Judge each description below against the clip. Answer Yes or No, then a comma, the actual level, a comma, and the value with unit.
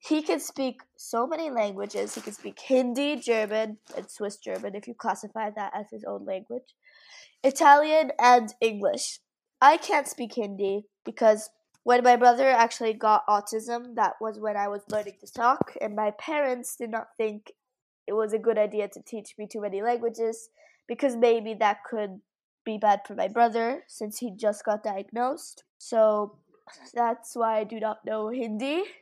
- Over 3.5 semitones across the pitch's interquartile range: No, average, 2.7 semitones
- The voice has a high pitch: Yes, high, 225 Hz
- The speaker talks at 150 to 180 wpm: Yes, average, 170 wpm